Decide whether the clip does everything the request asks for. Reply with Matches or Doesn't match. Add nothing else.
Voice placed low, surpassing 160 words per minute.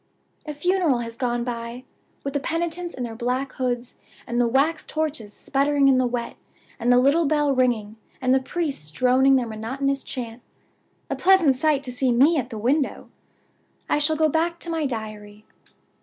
Doesn't match